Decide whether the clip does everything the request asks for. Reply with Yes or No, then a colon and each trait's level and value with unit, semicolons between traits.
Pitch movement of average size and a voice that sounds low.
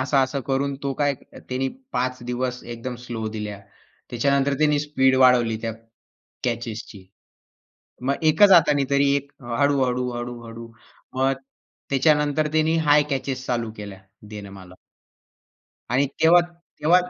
Yes: average, 3.2 semitones; low, 130 Hz